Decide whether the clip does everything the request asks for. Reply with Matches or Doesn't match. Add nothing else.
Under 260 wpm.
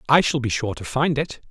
Doesn't match